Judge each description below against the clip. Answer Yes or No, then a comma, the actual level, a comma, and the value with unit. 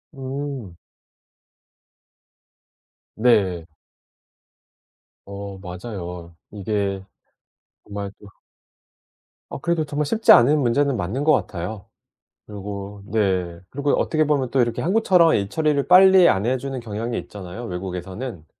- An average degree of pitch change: No, wide, 6.5 semitones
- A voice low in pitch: Yes, low, 110 Hz